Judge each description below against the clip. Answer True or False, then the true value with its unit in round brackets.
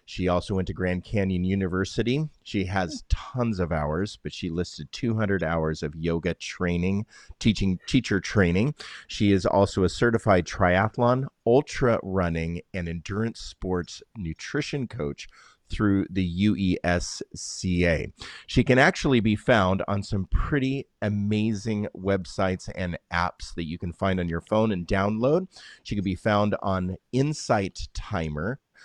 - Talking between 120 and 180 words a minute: True (140 wpm)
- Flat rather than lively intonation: False (3.6 semitones)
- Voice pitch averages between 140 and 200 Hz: False (95 Hz)